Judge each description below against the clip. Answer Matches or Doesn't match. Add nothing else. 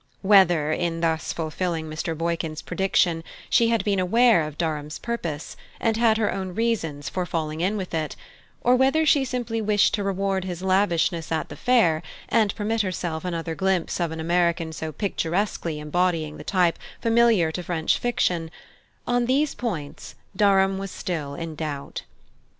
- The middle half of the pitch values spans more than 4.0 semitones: Matches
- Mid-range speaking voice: Matches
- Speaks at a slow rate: Doesn't match